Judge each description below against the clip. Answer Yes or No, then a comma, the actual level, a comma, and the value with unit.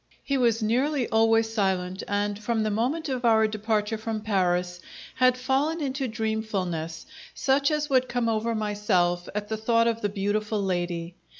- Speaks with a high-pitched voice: Yes, high, 220 Hz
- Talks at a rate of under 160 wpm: No, average, 165 wpm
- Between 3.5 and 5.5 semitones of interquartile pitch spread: No, average, 3.1 semitones